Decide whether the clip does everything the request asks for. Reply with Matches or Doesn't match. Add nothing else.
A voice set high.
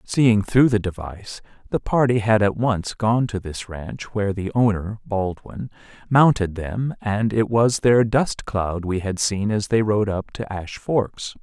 Doesn't match